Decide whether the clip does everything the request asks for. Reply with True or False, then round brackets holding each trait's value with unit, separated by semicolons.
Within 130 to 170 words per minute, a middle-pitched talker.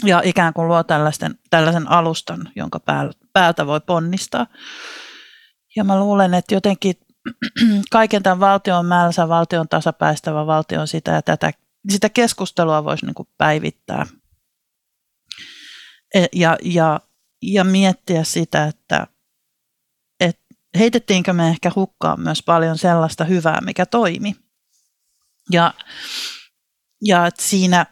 False (110 wpm; 175 Hz)